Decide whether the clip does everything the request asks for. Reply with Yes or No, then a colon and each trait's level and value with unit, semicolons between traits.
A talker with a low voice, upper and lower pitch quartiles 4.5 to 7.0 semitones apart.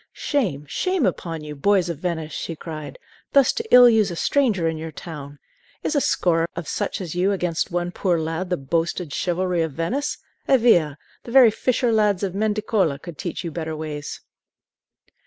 No: medium, 175 Hz; average, 4.9 semitones